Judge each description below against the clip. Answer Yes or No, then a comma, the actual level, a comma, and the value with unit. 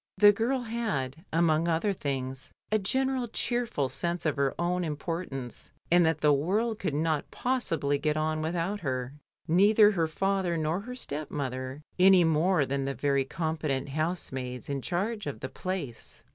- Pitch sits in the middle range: Yes, medium, 160 Hz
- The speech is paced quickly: No, average, 160 wpm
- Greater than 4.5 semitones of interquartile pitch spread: Yes, wide, 5.4 semitones